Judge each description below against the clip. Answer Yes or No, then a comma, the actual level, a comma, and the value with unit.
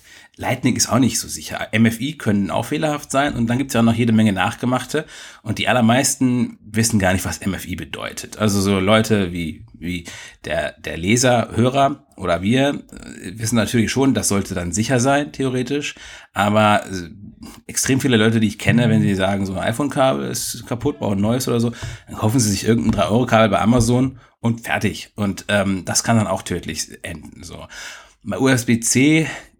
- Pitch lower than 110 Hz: No, low, 115 Hz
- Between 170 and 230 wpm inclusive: Yes, average, 180 wpm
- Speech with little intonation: No, average, 3.7 semitones